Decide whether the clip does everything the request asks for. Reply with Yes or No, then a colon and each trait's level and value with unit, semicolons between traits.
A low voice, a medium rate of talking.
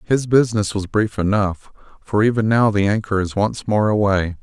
Yes: low, 105 Hz; average, 190 wpm